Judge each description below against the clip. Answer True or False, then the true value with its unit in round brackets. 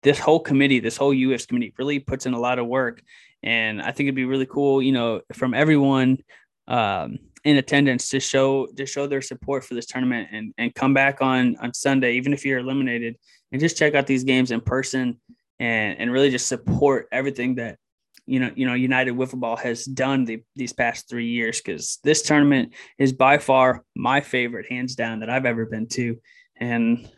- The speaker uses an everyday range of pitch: False (2.2 semitones)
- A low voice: True (130 Hz)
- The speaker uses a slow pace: False (205 wpm)